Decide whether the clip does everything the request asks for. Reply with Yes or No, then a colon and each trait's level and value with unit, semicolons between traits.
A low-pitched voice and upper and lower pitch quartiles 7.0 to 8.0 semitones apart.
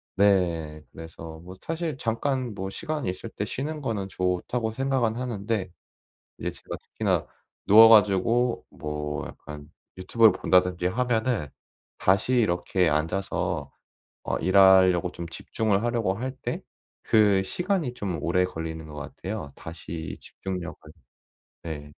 No: very low, 95 Hz; average, 5.2 semitones